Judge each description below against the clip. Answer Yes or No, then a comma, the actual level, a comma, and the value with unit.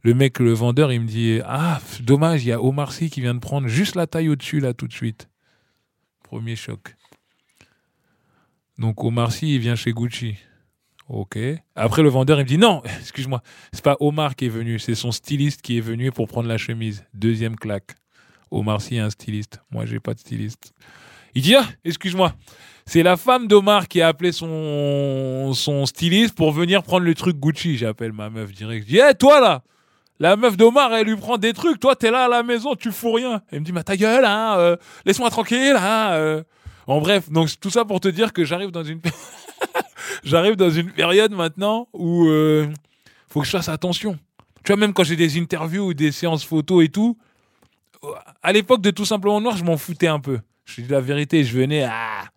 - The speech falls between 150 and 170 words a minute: No, average, 215 wpm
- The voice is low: No, medium, 155 Hz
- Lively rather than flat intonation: Yes, wide, 8.1 semitones